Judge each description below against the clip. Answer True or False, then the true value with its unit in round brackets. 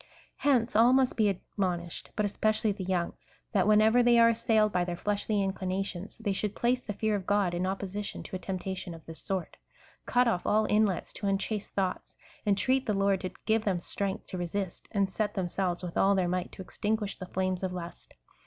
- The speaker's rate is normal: False (210 wpm)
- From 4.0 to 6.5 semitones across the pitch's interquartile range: False (2.7 semitones)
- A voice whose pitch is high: True (195 Hz)